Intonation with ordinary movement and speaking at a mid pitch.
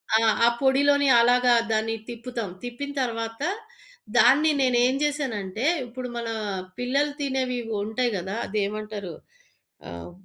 No: average, 3.2 semitones; high, 245 Hz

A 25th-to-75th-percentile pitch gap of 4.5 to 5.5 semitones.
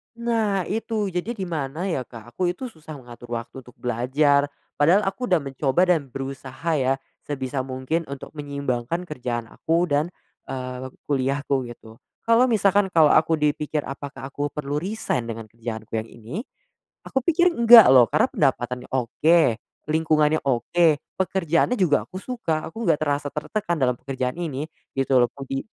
Yes: average, 5.1 semitones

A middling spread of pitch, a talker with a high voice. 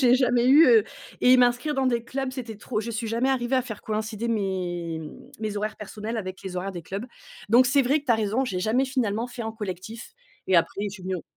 Yes: average, 4.0 semitones; high, 225 Hz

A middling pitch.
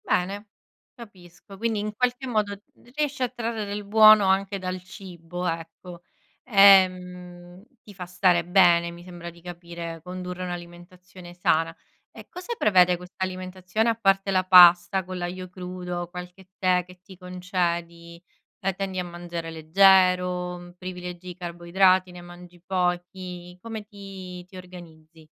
Yes: medium, 180 Hz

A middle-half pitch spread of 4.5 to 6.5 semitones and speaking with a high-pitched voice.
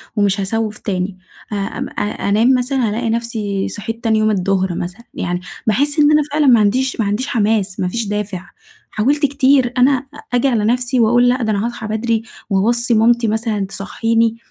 No: average, 3.1 semitones; high, 225 Hz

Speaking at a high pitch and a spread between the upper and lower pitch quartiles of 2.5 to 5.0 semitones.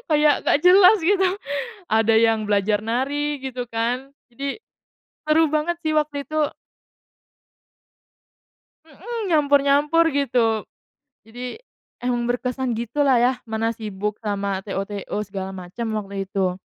No: high, 245 Hz; wide, 5.4 semitones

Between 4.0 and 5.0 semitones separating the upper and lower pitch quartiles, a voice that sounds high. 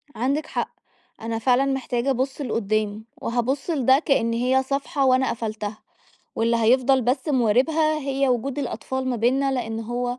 No: average, 2.8 semitones; very high, 255 Hz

